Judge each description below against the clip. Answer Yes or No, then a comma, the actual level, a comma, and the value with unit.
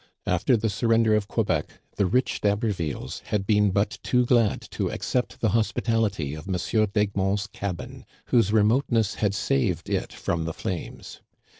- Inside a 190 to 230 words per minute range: No, average, 155 wpm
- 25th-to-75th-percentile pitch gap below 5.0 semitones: Yes, average, 2.9 semitones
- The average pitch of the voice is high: No, low, 105 Hz